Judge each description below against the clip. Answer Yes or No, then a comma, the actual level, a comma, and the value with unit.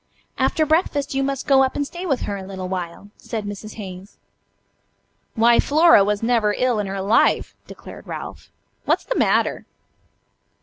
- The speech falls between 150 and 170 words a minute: Yes, average, 165 wpm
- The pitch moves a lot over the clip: Yes, wide, 5.7 semitones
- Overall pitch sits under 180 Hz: No, high, 225 Hz